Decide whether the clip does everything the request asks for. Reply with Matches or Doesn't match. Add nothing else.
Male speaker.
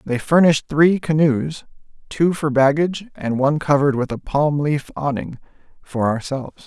Matches